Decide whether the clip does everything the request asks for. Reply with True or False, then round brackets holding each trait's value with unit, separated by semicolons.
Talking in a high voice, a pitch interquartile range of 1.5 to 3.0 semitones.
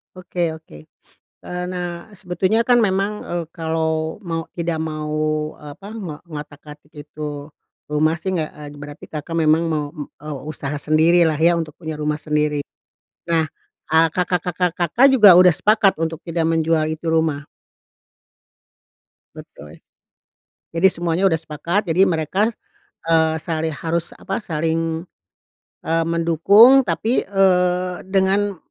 False (165 Hz; 2.7 semitones)